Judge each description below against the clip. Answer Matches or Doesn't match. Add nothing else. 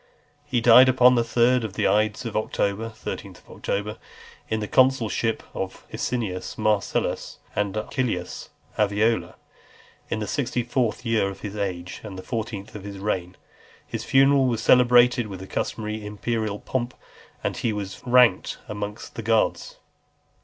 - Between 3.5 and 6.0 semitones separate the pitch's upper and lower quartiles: Doesn't match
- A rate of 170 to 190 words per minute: Doesn't match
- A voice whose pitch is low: Matches